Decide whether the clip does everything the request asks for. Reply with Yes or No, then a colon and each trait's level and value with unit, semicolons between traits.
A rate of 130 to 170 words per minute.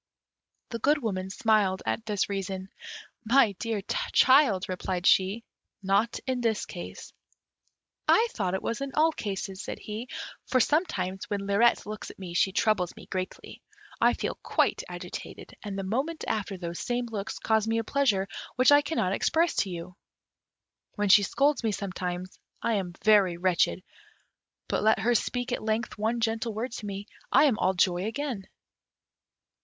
Yes: average, 165 wpm